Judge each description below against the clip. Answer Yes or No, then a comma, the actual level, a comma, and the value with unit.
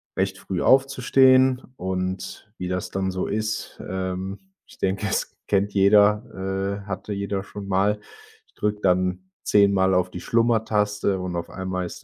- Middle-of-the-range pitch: No, low, 100 Hz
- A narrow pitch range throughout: Yes, narrow, 2.0 semitones